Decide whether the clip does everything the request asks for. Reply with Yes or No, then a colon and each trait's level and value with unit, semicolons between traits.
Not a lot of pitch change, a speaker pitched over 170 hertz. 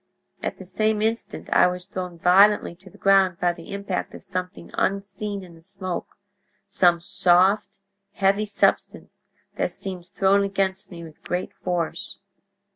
Yes: narrow, 1.9 semitones; high, 190 Hz